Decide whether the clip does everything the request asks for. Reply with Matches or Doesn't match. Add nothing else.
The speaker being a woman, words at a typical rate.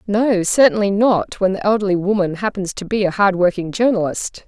Matches